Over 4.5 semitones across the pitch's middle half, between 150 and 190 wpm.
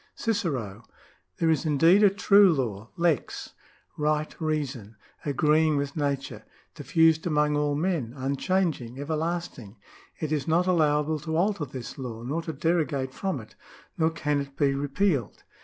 No: average, 3.3 semitones; average, 155 wpm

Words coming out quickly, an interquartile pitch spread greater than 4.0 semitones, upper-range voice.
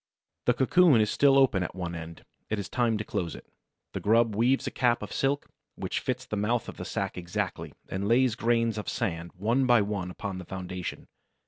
No: fast, 210 wpm; average, 4.7 semitones; low, 110 Hz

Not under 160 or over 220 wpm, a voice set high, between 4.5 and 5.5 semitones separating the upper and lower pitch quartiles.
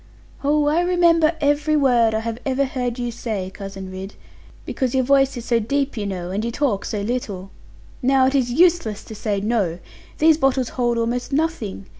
Yes: average, 190 wpm; high, 245 Hz; average, 4.8 semitones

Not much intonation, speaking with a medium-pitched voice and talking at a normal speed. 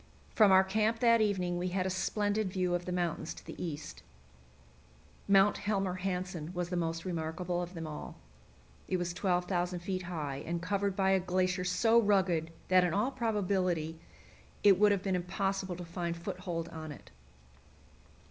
Yes: narrow, 2.0 semitones; medium, 180 Hz; average, 170 wpm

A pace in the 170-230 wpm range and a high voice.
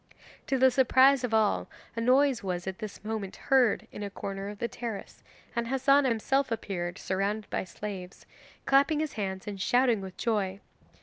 Yes: average, 175 wpm; high, 220 Hz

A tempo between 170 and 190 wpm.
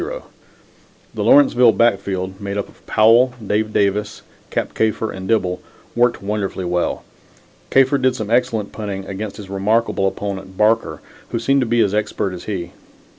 No: average, 155 wpm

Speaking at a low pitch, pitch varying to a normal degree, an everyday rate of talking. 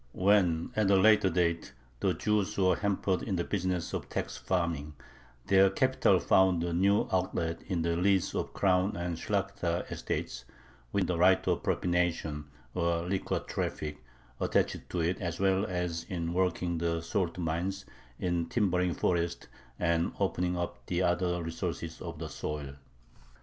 No: very low, 90 Hz; narrow, 2.1 semitones; average, 155 wpm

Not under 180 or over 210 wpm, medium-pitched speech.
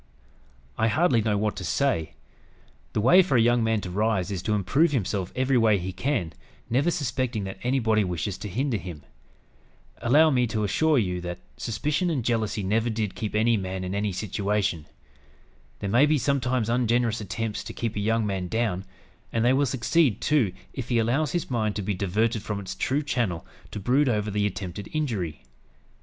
No: average, 190 wpm; low, 110 Hz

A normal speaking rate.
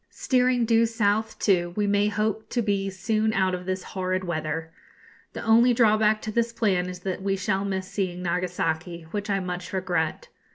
Yes: average, 180 wpm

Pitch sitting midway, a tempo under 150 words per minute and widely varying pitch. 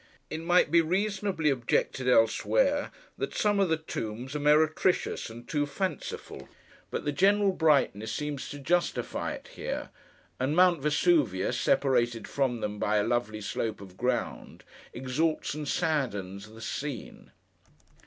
Yes: medium, 145 Hz; average, 140 wpm; wide, 6.1 semitones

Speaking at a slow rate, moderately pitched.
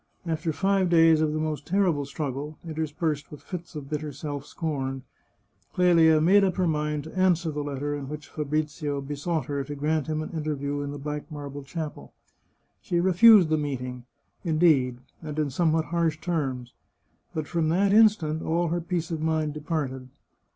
No: average, 170 wpm; medium, 155 Hz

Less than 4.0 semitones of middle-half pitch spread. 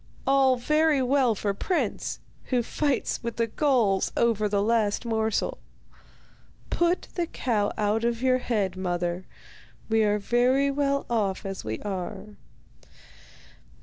No: average, 4.4 semitones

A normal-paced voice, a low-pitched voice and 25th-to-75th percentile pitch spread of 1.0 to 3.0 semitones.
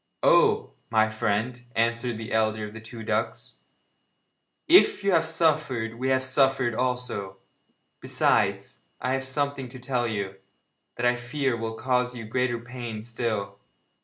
Yes: average, 145 wpm; low, 120 Hz; average, 2.7 semitones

